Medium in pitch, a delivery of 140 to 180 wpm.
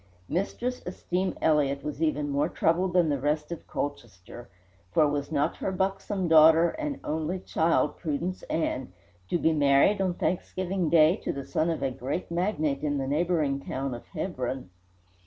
Yes: medium, 155 Hz; average, 165 wpm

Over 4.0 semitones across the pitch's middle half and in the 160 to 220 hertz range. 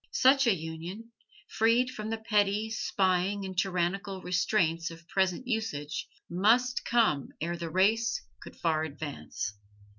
Yes: average, 4.9 semitones; high, 190 Hz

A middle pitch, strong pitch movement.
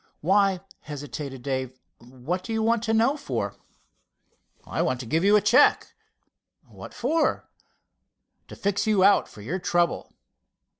Yes: medium, 180 Hz; wide, 7.8 semitones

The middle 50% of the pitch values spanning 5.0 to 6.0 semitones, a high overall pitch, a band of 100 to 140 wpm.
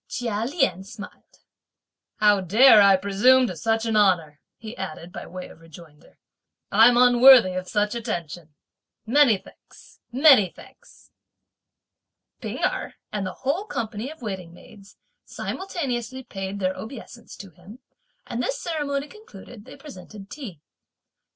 Yes: average, 5.3 semitones; high, 215 Hz; slow, 135 wpm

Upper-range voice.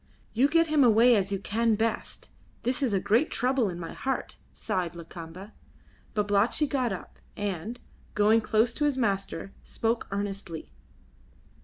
Yes: high, 215 Hz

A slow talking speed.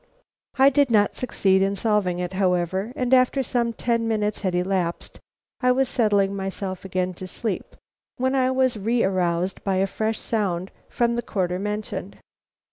No: average, 165 wpm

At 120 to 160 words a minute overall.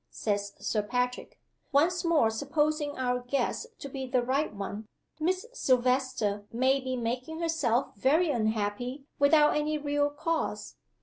Yes: slow, 135 wpm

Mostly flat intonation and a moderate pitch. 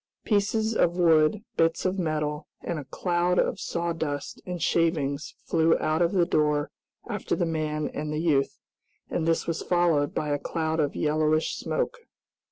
Yes: narrow, 2.3 semitones; medium, 160 Hz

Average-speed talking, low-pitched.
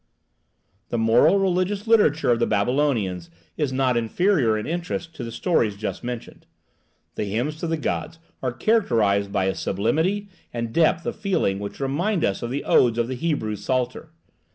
Yes: average, 170 wpm; low, 130 Hz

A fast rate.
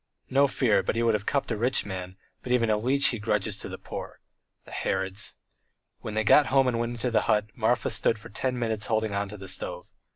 Yes: fast, 235 wpm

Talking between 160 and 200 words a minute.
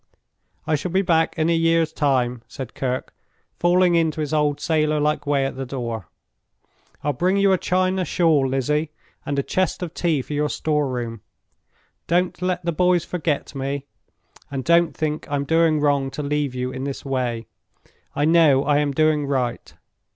Yes: average, 180 wpm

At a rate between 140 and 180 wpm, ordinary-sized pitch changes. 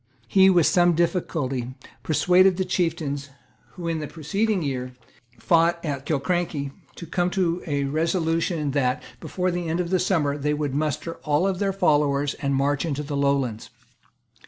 Yes: average, 160 wpm; average, 3.8 semitones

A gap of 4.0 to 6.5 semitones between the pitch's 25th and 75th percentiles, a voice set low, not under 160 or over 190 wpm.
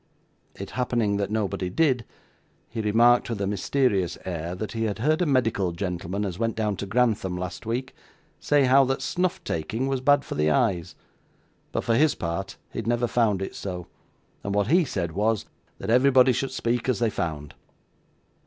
Yes: average, 4.7 semitones; low, 110 Hz; average, 185 wpm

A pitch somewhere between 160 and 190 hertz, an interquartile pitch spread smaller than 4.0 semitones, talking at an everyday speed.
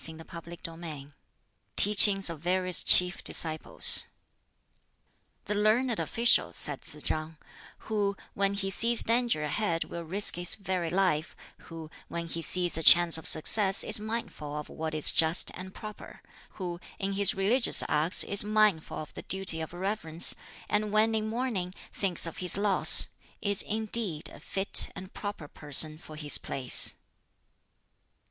No: medium, 185 Hz; average, 4.4 semitones; average, 150 wpm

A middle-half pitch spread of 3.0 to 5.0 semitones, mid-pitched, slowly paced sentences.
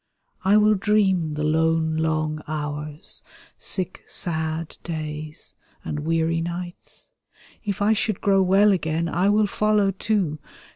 Yes: average, 4.0 semitones; medium, 165 Hz; slow, 130 wpm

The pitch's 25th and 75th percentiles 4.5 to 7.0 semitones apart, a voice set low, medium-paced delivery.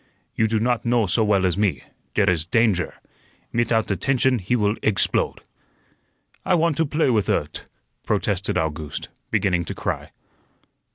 Yes: average, 4.8 semitones; low, 110 Hz; average, 150 wpm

